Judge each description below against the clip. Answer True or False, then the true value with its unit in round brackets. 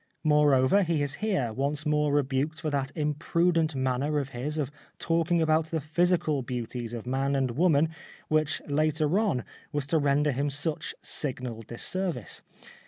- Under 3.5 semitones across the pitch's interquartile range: True (2.9 semitones)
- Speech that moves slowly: False (155 wpm)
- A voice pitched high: False (150 Hz)